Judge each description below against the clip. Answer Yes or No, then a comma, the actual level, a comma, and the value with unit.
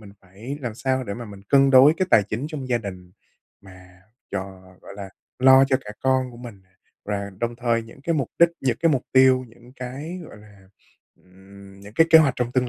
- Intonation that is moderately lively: Yes, average, 4.9 semitones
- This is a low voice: Yes, low, 120 Hz